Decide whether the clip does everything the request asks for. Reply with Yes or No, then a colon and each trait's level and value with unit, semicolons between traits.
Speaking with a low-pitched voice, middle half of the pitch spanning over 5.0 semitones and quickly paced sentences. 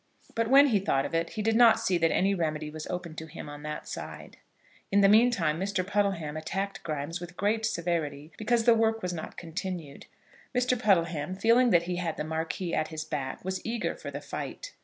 No: medium, 180 Hz; wide, 5.4 semitones; fast, 210 wpm